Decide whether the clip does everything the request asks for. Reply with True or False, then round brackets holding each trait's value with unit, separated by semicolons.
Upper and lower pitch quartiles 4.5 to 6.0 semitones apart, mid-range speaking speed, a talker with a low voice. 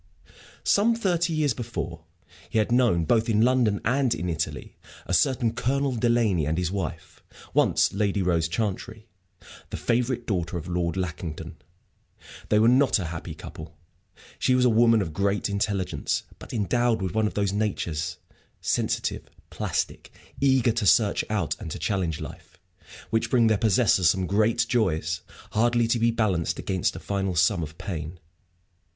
True (5.1 semitones; 160 wpm; 105 Hz)